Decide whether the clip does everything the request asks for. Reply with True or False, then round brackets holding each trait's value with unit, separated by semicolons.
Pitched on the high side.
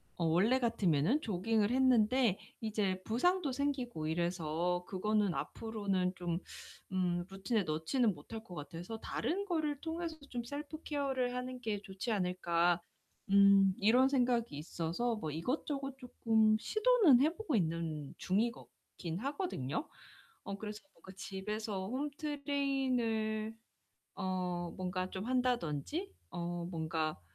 True (215 Hz)